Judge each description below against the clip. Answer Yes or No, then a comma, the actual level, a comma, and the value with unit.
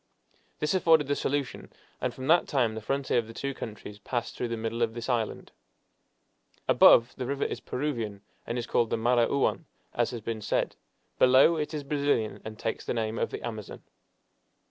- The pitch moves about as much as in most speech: Yes, average, 3.7 semitones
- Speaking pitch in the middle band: No, low, 120 Hz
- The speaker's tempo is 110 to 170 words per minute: No, average, 190 wpm